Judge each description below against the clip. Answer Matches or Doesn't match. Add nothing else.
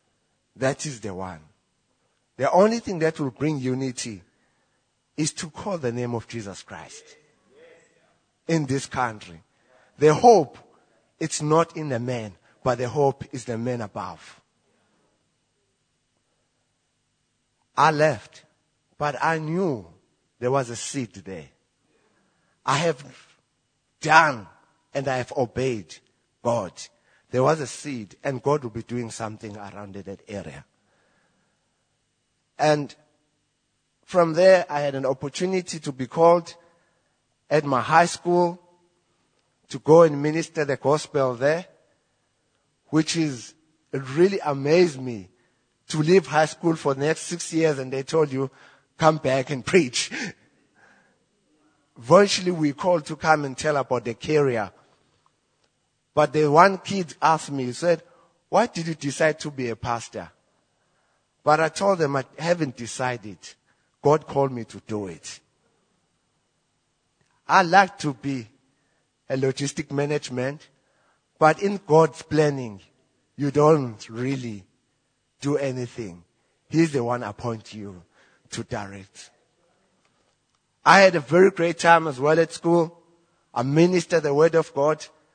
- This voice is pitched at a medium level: Matches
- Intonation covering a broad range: Doesn't match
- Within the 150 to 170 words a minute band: Doesn't match